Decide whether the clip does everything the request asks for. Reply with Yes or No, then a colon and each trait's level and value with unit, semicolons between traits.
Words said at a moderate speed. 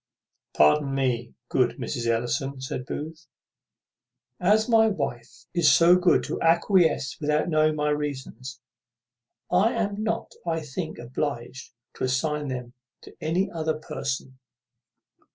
No: slow, 125 wpm